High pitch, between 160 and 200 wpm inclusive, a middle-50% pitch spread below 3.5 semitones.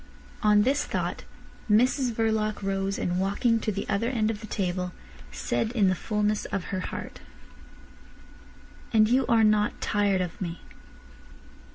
No: high, 210 Hz; average, 150 wpm; narrow, 2.5 semitones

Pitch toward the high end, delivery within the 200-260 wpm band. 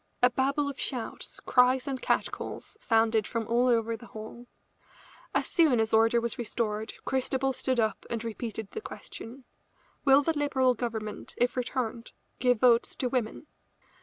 No: high, 240 Hz; average, 155 wpm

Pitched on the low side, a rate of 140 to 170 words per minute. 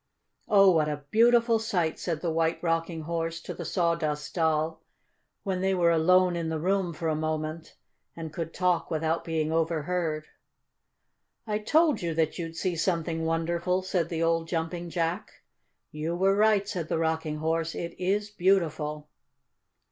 No: medium, 165 Hz; average, 160 wpm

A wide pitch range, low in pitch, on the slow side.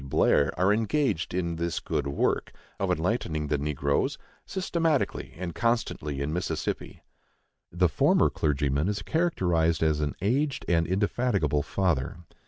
Yes: wide, 6.1 semitones; very low, 85 Hz; slow, 130 wpm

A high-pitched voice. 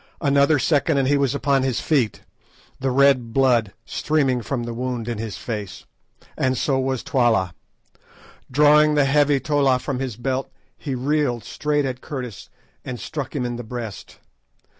No: low, 130 Hz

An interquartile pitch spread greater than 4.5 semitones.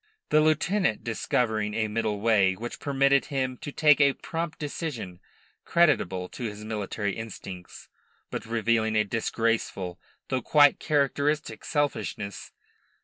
Yes: wide, 5.4 semitones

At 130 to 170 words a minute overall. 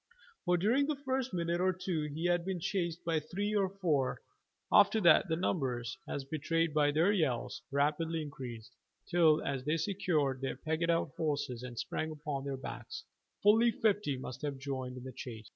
No: average, 180 wpm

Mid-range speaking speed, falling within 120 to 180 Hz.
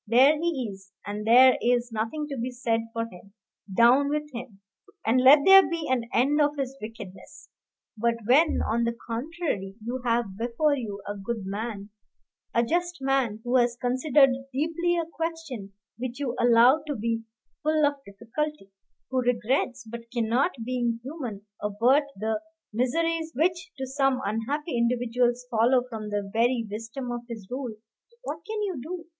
No: average, 160 wpm; high, 245 Hz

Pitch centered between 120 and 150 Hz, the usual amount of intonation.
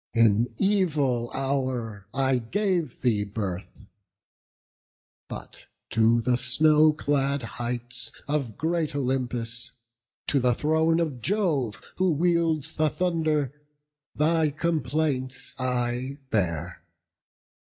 Yes: low, 135 Hz; average, 4.6 semitones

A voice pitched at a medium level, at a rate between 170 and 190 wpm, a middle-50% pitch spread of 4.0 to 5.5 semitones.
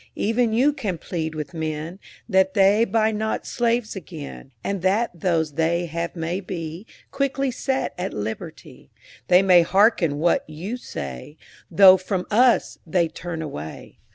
No: medium, 180 Hz; average, 150 wpm; average, 5.1 semitones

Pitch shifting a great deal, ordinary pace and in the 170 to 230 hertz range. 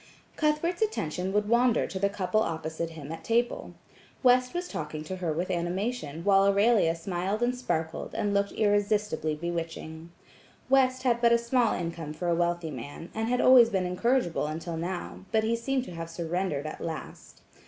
Yes: wide, 6.1 semitones; average, 175 wpm; high, 190 Hz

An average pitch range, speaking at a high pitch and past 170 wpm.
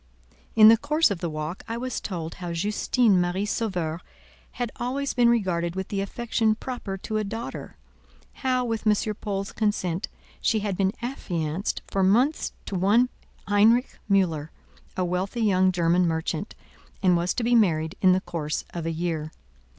No: average, 4.5 semitones; high, 195 Hz; average, 165 wpm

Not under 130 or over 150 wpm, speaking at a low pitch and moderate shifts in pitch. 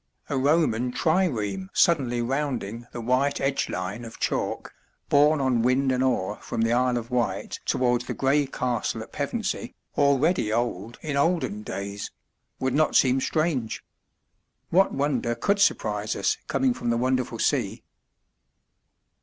Yes: average, 145 wpm; low, 130 Hz; average, 3.5 semitones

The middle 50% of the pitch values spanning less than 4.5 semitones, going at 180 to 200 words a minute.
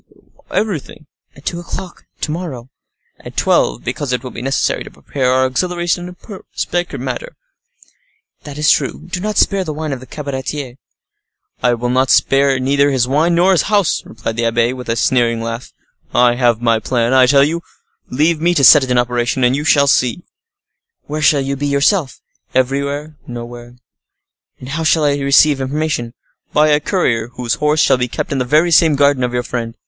Yes: average, 3.8 semitones; average, 190 wpm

